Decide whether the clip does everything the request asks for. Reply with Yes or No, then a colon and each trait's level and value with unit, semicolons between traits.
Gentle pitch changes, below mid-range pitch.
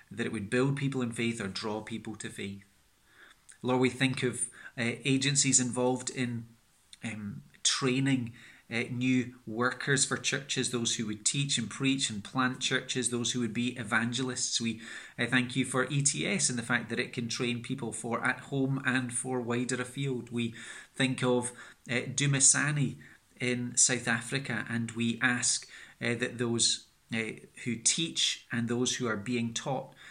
Yes: narrow, 1.8 semitones; low, 125 Hz